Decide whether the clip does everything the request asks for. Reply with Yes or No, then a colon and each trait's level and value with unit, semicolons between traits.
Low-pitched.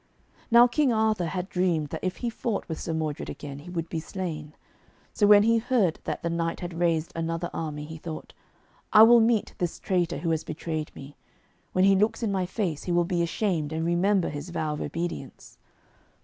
No: medium, 175 Hz